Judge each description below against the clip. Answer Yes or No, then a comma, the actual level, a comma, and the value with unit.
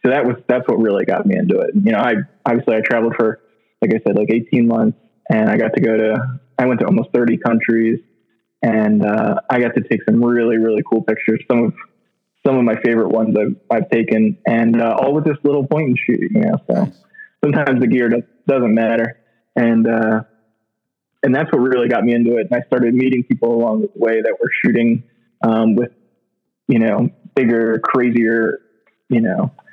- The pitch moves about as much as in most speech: No, narrow, 2.2 semitones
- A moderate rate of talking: No, fast, 210 wpm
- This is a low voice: Yes, low, 115 Hz